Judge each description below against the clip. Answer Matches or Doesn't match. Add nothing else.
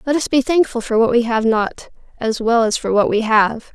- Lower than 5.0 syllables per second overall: Doesn't match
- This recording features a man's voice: Doesn't match